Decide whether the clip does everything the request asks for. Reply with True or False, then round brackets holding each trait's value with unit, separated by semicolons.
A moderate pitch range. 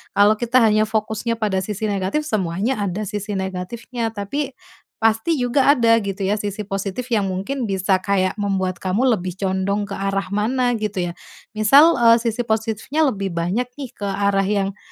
True (3.1 semitones)